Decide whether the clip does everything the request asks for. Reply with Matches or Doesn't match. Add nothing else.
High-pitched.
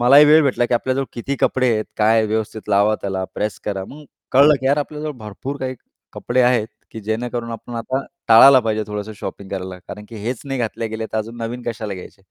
Doesn't match